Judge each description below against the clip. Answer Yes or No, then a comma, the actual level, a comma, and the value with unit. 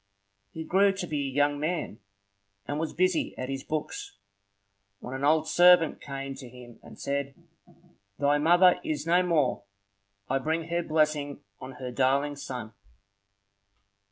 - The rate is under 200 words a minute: Yes, average, 150 wpm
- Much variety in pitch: No, average, 3.3 semitones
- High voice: No, medium, 145 Hz